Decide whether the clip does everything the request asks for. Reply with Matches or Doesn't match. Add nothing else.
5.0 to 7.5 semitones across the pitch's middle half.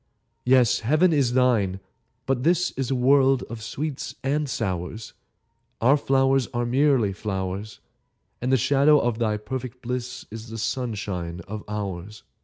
Doesn't match